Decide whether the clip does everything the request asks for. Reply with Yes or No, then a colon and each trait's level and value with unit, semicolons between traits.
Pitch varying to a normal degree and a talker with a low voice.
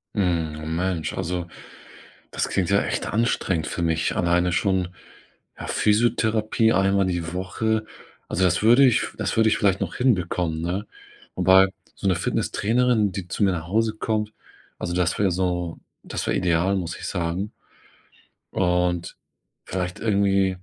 Yes: average, 3.2 semitones; very low, 95 Hz